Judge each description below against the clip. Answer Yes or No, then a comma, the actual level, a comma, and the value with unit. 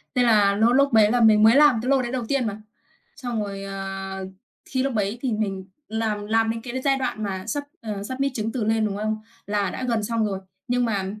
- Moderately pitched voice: No, high, 220 Hz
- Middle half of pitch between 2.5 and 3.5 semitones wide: Yes, average, 3.1 semitones